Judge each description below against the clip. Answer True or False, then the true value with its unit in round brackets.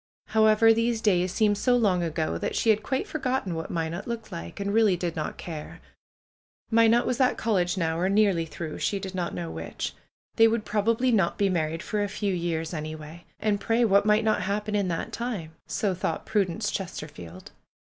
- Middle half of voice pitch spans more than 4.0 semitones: True (4.6 semitones)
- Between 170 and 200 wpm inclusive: True (195 wpm)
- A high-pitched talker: True (200 Hz)